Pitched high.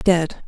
No: medium, 170 Hz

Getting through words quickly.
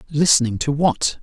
No: average, 145 wpm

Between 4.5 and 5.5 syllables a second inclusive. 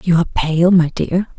Yes: 5.0 syllables/s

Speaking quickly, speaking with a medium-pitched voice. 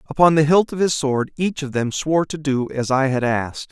Yes: fast, 260 wpm; medium, 145 Hz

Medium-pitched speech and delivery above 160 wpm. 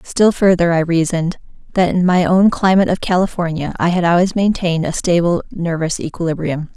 Yes: medium, 175 Hz; average, 170 wpm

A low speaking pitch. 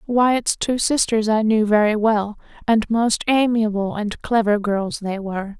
No: high, 220 Hz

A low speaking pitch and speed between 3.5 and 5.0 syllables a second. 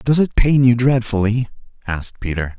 No: low, 115 Hz; 5.2 syllables/s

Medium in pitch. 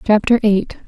No: high, 210 Hz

